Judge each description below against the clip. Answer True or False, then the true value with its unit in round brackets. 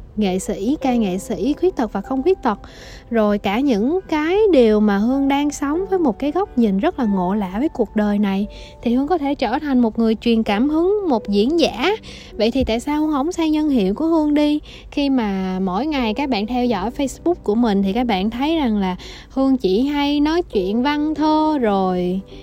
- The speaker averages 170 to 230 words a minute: True (225 wpm)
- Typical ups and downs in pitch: False (6.0 semitones)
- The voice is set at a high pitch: True (255 Hz)